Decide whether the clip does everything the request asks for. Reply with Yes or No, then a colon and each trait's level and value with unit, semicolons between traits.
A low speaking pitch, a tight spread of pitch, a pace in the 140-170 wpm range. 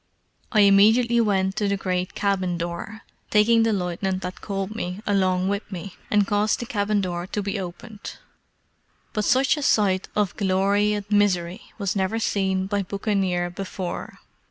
No: high, 200 Hz; narrow, 2.1 semitones; average, 160 wpm